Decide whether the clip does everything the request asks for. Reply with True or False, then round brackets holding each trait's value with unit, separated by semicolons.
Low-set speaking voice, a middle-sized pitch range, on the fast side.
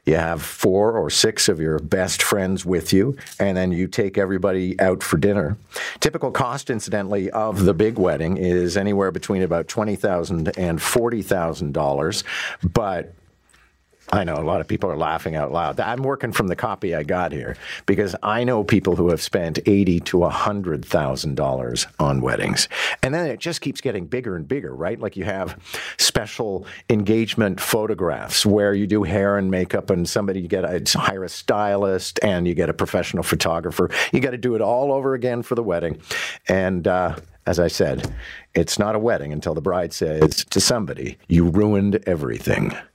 False (95 Hz; 3.2 semitones; 185 wpm)